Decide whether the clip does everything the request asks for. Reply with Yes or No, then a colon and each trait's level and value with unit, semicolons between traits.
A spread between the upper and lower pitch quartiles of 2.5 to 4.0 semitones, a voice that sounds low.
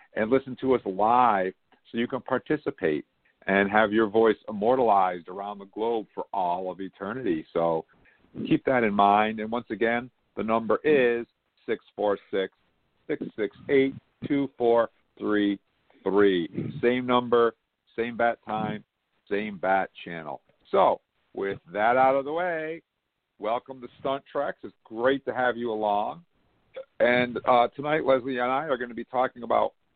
Yes: average, 3.7 semitones; low, 115 Hz